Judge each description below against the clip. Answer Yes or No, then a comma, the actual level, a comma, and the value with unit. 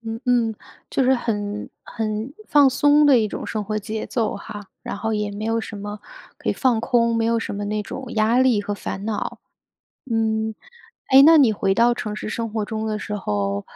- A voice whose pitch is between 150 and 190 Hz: No, high, 220 Hz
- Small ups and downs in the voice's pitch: Yes, narrow, 2.2 semitones